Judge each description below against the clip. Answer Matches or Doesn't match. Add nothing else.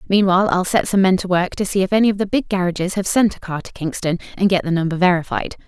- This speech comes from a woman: Matches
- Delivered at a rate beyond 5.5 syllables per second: Matches